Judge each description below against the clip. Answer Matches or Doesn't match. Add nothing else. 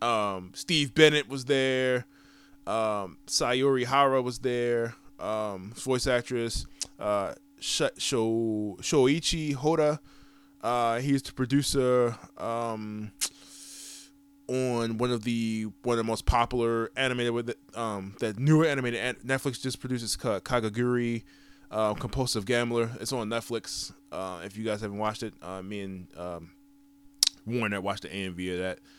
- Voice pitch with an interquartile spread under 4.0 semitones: Doesn't match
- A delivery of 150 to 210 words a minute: Doesn't match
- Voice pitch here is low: Matches